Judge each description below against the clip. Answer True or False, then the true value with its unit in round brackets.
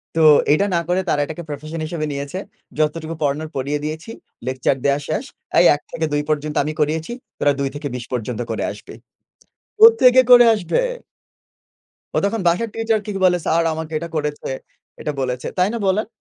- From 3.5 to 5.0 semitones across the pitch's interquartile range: True (4.1 semitones)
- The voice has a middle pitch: True (155 Hz)